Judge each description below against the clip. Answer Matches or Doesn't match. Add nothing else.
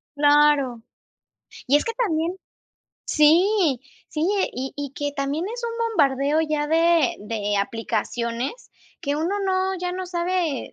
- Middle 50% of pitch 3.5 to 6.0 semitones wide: Matches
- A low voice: Doesn't match